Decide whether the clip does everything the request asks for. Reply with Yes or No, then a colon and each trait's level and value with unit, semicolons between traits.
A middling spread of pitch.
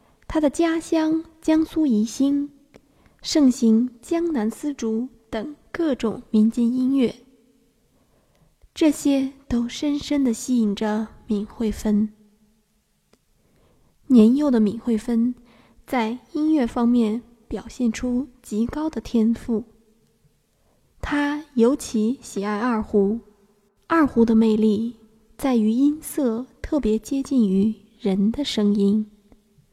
Yes: average, 4.2 semitones